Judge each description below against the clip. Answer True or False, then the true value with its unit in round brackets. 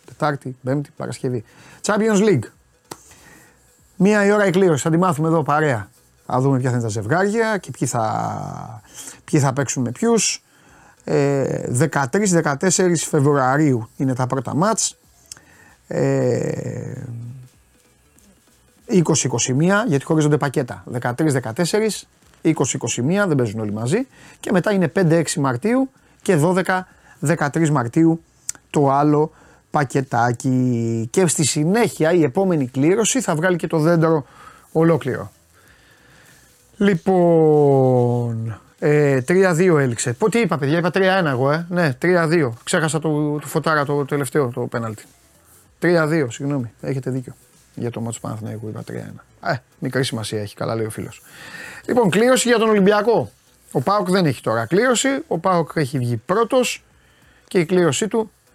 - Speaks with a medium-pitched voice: True (150 Hz)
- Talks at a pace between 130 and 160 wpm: True (135 wpm)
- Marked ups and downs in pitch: True (6.1 semitones)